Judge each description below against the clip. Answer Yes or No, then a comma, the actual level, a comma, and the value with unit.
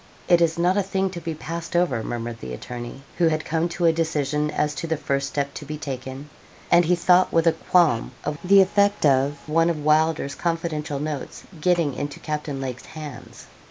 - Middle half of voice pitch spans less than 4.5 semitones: Yes, average, 3.2 semitones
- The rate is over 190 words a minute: Yes, average, 200 wpm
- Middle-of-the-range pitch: Yes, medium, 155 Hz